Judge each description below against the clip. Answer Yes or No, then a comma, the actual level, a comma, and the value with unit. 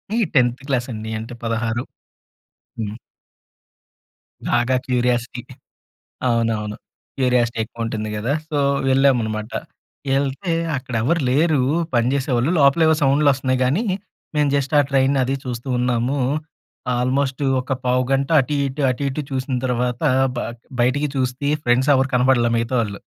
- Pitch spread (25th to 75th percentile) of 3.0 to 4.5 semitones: No, narrow, 2.4 semitones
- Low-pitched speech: Yes, low, 125 Hz